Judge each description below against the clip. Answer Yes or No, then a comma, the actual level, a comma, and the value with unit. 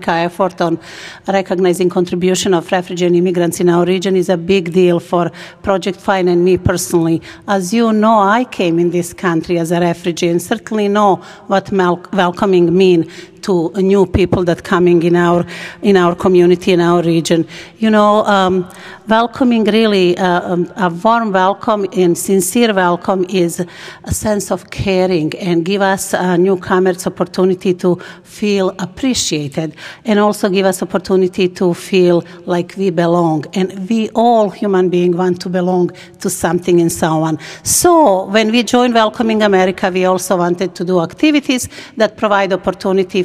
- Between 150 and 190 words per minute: Yes, average, 160 wpm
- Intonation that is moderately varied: No, narrow, 2.1 semitones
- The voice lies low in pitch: No, medium, 185 Hz